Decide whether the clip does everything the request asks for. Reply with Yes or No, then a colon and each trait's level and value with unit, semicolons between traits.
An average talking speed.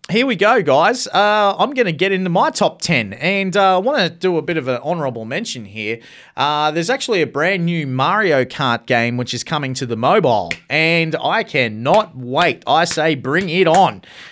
No: fast, 210 wpm